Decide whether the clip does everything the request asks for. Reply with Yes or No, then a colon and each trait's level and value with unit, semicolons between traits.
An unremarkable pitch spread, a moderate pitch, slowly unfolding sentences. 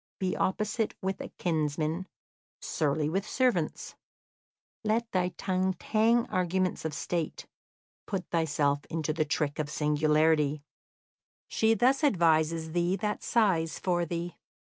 Yes: average, 3.9 semitones; medium, 175 Hz; slow, 120 wpm